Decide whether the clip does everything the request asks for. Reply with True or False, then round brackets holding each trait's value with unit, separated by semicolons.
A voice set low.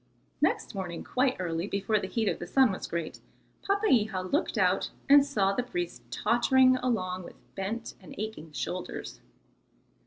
False (210 Hz)